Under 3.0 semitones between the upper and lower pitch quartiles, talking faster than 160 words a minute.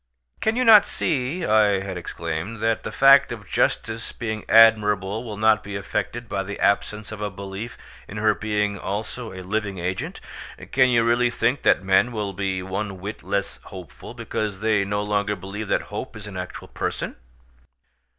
Yes: narrow, 2.4 semitones; average, 180 wpm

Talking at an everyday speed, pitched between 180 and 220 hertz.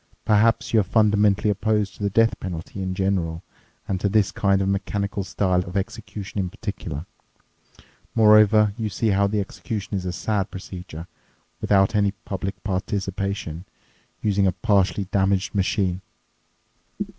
No: average, 145 wpm; low, 100 Hz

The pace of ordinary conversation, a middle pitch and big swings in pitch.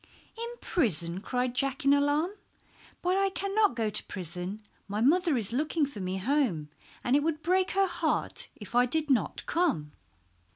No: average, 170 wpm; very high, 275 Hz; wide, 8.2 semitones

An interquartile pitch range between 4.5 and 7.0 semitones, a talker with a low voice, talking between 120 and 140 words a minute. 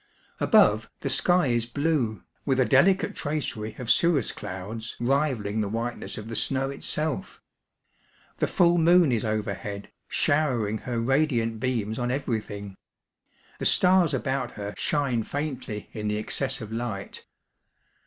Yes: average, 4.8 semitones; low, 120 Hz; slow, 135 wpm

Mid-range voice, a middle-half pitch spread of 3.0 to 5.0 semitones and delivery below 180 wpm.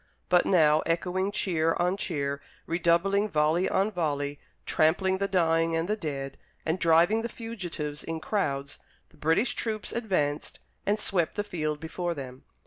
Yes: medium, 170 Hz; average, 4.2 semitones; average, 150 wpm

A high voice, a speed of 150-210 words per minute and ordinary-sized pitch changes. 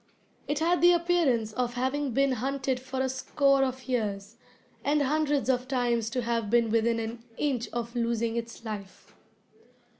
Yes: very high, 250 Hz; average, 160 wpm; average, 3.1 semitones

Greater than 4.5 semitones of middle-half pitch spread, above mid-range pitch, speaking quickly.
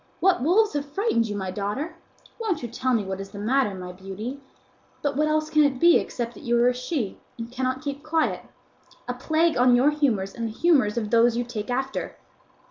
Yes: average, 5.0 semitones; very high, 250 Hz; fast, 215 wpm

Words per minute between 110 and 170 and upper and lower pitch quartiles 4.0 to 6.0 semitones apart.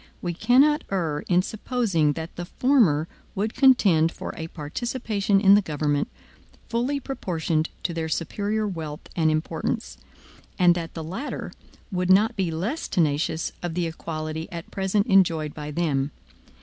Yes: average, 150 wpm; average, 4.5 semitones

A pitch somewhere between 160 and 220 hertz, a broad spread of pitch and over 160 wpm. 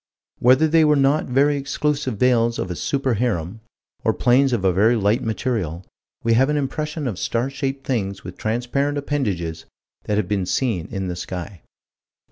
No: low, 120 Hz; wide, 5.9 semitones; average, 175 wpm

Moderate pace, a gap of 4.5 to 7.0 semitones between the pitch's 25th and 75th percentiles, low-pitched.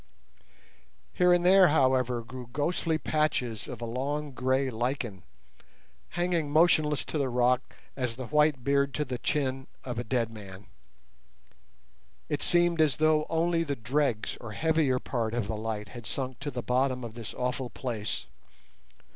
No: average, 155 wpm; average, 4.1 semitones; low, 130 Hz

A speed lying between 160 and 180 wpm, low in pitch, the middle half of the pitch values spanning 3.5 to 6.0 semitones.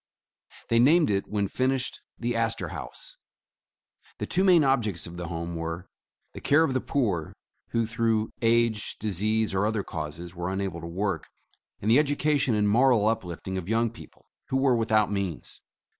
Yes: average, 165 wpm; low, 110 Hz; average, 4.4 semitones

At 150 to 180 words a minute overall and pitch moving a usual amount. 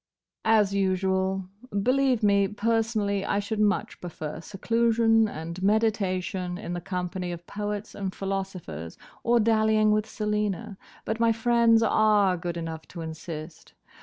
No: slow, 135 wpm; average, 3.3 semitones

